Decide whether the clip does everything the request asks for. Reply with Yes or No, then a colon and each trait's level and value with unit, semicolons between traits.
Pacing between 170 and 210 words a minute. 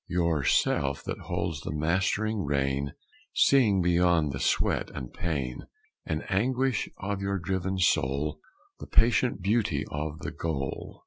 No: slow, 135 wpm